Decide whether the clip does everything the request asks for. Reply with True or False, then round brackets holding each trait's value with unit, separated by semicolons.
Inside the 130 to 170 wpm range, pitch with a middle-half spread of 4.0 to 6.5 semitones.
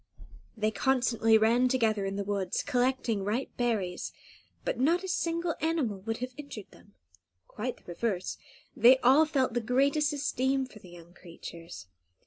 True (155 wpm; 4.7 semitones)